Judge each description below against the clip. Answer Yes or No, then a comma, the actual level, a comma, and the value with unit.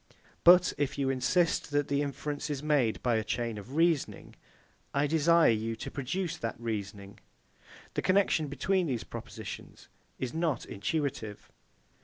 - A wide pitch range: Yes, wide, 5.7 semitones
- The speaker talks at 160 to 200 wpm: No, average, 145 wpm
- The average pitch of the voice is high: No, medium, 140 Hz